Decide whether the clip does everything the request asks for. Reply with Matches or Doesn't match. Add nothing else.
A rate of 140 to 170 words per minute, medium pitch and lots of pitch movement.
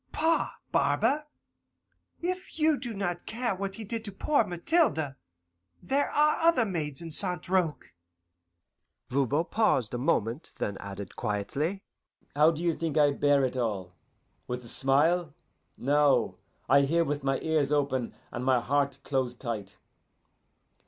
Matches